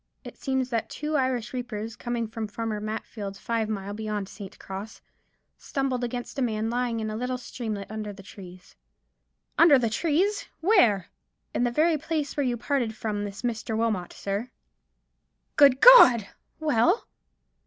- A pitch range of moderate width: Yes, average, 3.6 semitones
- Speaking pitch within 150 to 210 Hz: No, high, 230 Hz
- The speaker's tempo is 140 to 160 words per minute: Yes, average, 155 wpm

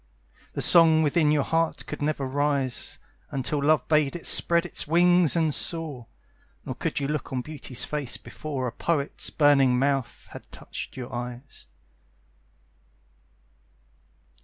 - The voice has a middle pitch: Yes, medium, 145 Hz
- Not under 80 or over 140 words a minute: Yes, slow, 135 wpm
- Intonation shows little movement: No, average, 3.1 semitones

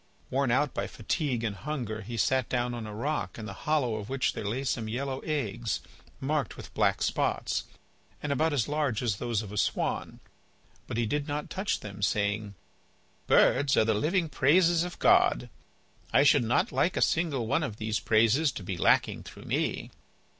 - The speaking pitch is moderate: No, low, 125 Hz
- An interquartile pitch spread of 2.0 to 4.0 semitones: No, average, 5.3 semitones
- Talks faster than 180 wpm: Yes, average, 190 wpm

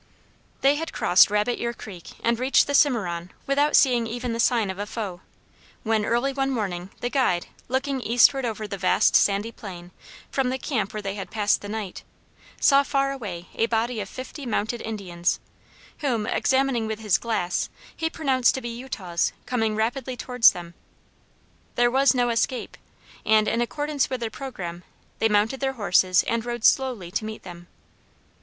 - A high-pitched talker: Yes, high, 230 Hz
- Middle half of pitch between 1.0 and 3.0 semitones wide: No, average, 4.2 semitones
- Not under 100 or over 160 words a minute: No, average, 175 wpm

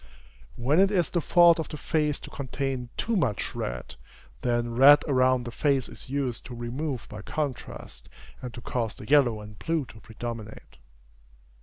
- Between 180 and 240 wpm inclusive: No, average, 170 wpm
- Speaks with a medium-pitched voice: No, low, 130 Hz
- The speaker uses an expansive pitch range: No, average, 3.9 semitones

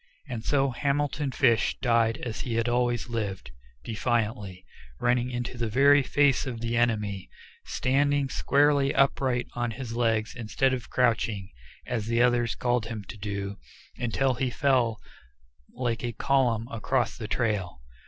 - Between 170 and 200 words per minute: No, average, 145 wpm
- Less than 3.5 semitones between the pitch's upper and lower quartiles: Yes, average, 2.7 semitones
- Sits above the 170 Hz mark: No, low, 120 Hz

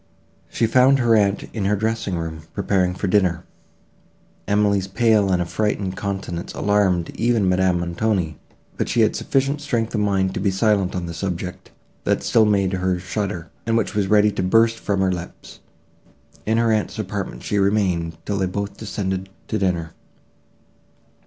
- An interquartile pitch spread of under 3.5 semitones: Yes, average, 2.8 semitones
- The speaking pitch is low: Yes, low, 100 Hz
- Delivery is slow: No, average, 165 wpm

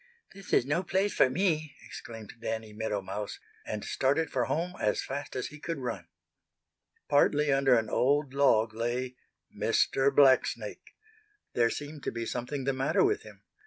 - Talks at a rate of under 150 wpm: No, average, 160 wpm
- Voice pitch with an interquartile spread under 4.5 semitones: Yes, average, 4.1 semitones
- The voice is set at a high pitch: No, low, 135 Hz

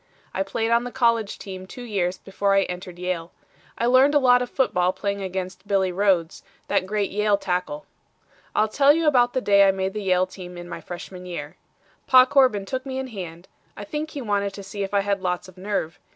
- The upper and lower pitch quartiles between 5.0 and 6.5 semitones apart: No, average, 4.6 semitones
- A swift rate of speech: Yes, fast, 220 wpm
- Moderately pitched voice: No, high, 200 Hz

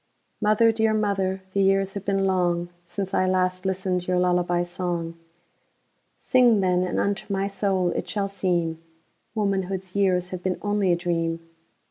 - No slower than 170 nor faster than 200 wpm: No, average, 140 wpm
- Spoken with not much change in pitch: Yes, narrow, 2.0 semitones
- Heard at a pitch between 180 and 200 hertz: Yes, medium, 185 Hz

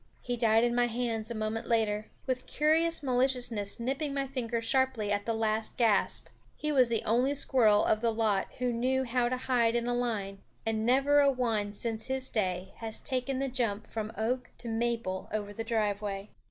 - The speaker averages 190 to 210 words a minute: Yes, average, 195 wpm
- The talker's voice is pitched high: Yes, high, 235 Hz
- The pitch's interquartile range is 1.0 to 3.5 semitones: Yes, average, 2.8 semitones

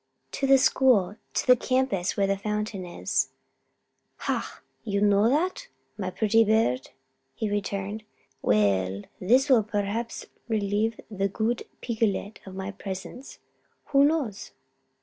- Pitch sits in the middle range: No, high, 210 Hz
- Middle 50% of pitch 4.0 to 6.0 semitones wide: No, average, 3.3 semitones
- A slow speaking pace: Yes, slow, 130 wpm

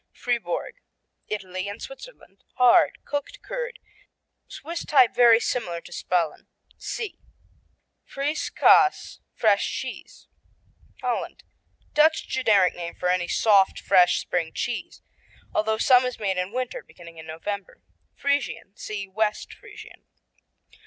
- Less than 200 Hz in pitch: No, high, 215 Hz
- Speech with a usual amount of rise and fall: No, wide, 6.8 semitones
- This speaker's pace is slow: Yes, slow, 120 wpm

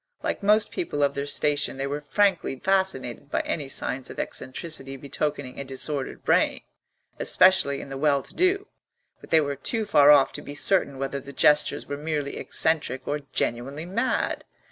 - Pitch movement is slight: No, average, 3.3 semitones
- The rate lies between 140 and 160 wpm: No, average, 175 wpm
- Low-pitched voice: No, medium, 145 Hz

